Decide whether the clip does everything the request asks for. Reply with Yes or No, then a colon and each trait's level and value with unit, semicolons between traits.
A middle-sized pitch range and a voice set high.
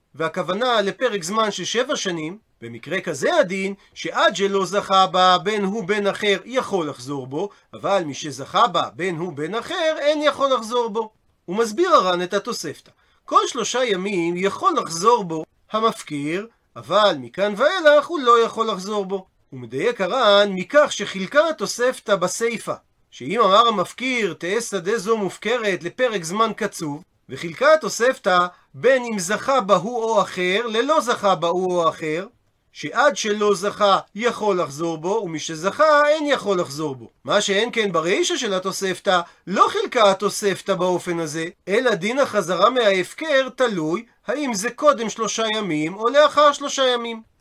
Yes: average, 4.9 semitones; high, 205 Hz